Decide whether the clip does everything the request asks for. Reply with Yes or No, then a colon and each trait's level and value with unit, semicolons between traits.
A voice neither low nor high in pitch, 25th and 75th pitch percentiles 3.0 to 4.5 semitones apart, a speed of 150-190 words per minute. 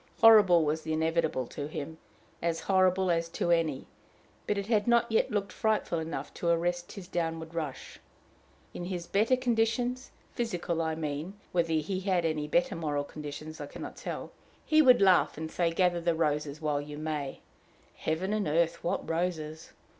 Yes: medium, 170 Hz; average, 3.6 semitones; average, 175 wpm